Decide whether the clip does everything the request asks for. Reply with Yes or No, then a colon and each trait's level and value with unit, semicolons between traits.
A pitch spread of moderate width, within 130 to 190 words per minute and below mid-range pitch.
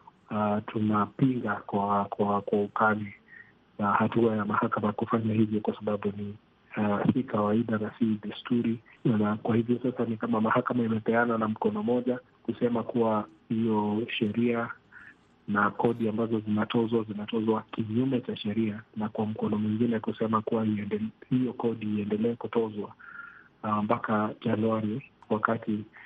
No: narrow, 1.7 semitones; average, 135 wpm; low, 110 Hz